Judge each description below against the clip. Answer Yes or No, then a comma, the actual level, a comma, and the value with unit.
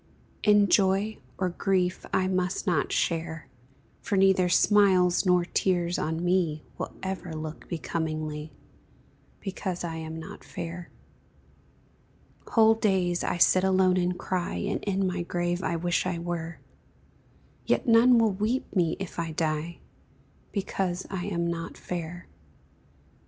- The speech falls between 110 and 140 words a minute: Yes, slow, 135 wpm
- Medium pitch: Yes, medium, 180 Hz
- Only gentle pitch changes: Yes, narrow, 2.2 semitones